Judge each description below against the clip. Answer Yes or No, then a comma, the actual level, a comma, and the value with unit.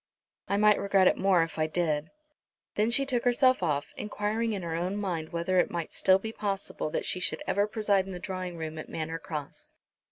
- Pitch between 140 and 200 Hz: Yes, medium, 185 Hz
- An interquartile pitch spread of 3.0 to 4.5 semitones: Yes, average, 4.1 semitones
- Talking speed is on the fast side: Yes, fast, 215 wpm